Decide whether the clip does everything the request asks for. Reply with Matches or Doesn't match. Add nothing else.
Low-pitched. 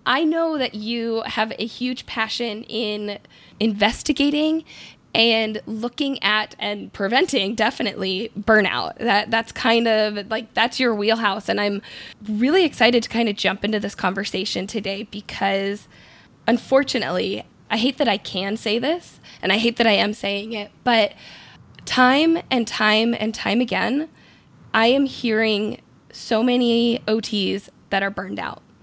Doesn't match